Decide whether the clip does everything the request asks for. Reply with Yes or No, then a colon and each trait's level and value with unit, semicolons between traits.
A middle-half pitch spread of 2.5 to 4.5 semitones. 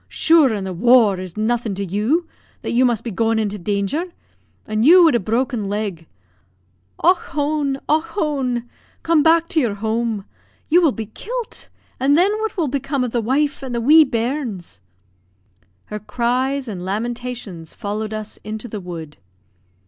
No: wide, 5.5 semitones